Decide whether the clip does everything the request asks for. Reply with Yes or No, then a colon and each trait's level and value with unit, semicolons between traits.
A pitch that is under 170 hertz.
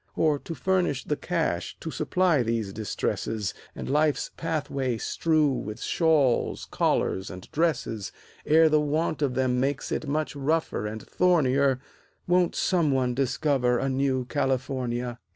Yes: medium, 140 Hz